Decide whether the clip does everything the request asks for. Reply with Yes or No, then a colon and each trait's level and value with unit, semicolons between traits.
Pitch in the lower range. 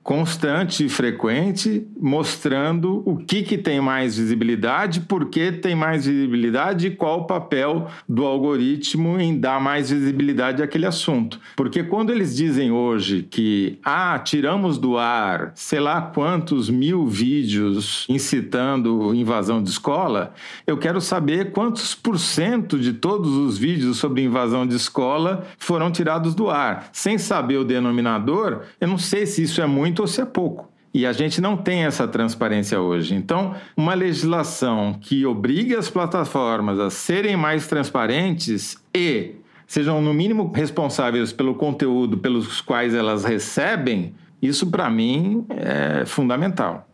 No: medium, 150 Hz